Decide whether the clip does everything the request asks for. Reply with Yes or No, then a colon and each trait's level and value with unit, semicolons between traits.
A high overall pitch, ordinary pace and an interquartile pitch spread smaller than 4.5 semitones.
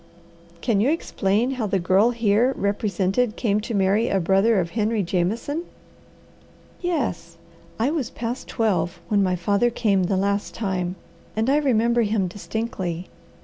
Yes: high, 210 Hz; average, 145 wpm; average, 3.5 semitones